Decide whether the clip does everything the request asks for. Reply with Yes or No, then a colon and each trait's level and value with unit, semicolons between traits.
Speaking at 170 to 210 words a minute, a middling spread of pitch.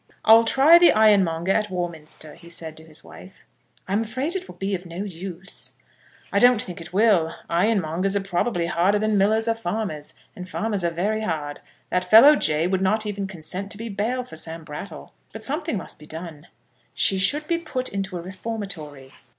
Yes: average, 190 wpm; average, 4.4 semitones